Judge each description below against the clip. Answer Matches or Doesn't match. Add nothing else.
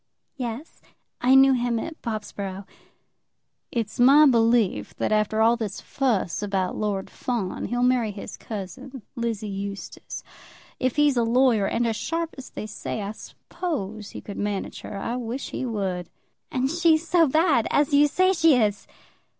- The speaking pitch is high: Matches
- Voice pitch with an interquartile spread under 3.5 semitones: Doesn't match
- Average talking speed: Matches